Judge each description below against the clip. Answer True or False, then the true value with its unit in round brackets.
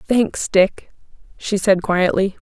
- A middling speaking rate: False (95 wpm)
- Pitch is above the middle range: True (195 Hz)